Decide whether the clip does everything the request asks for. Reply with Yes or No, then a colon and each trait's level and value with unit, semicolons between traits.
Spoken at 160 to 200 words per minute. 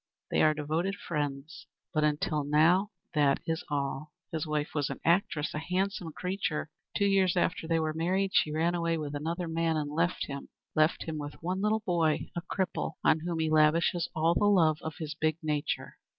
Yes: average, 195 wpm